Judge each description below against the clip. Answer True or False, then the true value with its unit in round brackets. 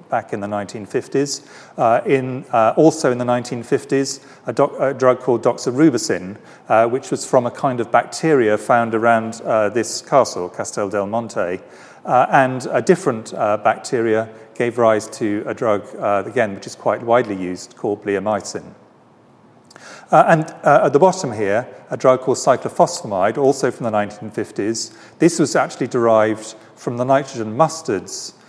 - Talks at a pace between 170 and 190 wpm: False (160 wpm)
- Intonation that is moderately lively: True (3.8 semitones)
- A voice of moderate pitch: False (120 Hz)